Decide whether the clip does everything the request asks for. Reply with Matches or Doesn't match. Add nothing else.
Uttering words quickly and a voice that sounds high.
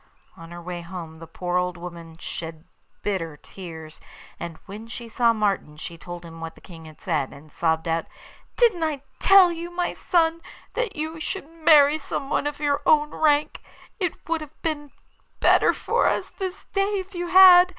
Doesn't match